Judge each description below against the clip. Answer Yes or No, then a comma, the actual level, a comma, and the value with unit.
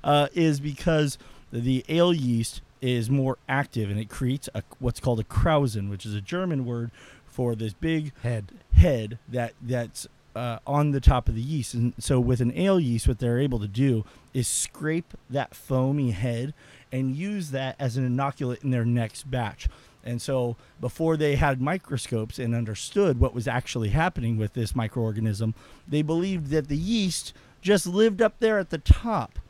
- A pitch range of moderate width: Yes, average, 3.8 semitones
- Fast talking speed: No, average, 185 wpm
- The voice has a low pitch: Yes, low, 130 Hz